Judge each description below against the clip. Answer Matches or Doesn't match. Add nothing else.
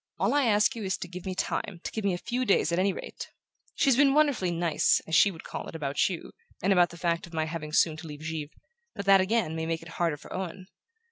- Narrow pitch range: Doesn't match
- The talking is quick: Matches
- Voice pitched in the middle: Matches